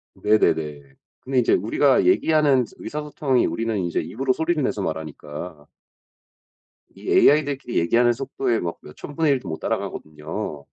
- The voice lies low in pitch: Yes, low, 120 Hz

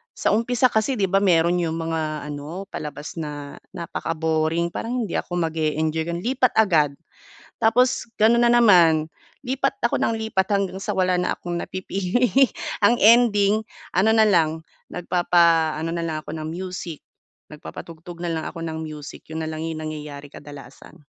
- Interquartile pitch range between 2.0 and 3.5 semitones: No, average, 4.5 semitones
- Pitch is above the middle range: No, medium, 170 Hz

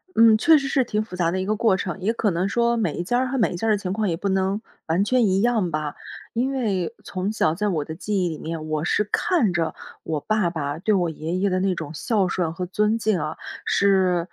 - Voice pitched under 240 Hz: Yes, high, 190 Hz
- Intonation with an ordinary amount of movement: Yes, average, 4.2 semitones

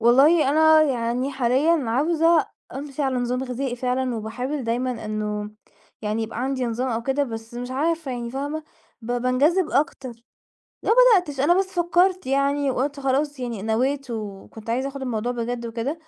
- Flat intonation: No, average, 3.5 semitones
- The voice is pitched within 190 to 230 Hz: No, very high, 260 Hz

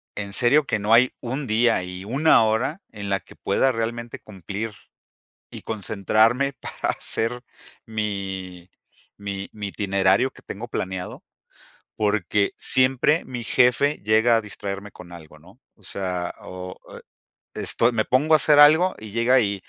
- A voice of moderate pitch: No, low, 110 Hz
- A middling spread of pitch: Yes, average, 4.0 semitones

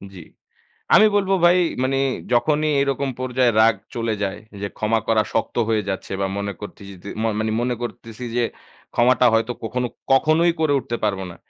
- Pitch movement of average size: Yes, average, 3.6 semitones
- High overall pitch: No, low, 120 Hz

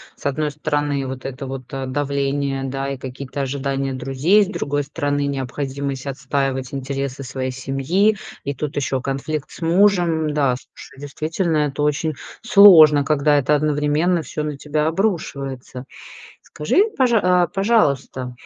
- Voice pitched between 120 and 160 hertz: Yes, medium, 140 Hz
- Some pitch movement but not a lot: No, narrow, 2.3 semitones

